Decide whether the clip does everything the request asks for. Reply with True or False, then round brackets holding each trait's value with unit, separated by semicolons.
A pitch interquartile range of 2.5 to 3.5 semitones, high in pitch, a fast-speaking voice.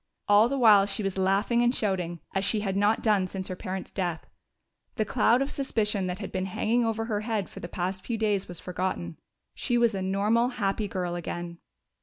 True (3.1 semitones; 200 Hz; 210 wpm)